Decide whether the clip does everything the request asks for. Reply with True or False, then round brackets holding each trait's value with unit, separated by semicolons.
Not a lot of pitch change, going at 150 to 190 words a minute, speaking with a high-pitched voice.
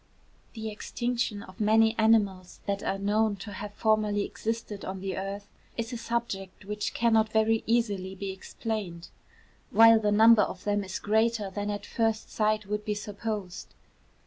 True (2.0 semitones; 160 wpm; 210 Hz)